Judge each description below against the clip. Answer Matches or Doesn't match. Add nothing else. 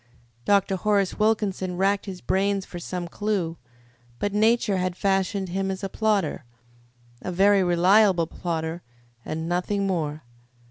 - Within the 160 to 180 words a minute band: Doesn't match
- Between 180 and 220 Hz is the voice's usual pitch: Matches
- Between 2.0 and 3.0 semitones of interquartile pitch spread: Matches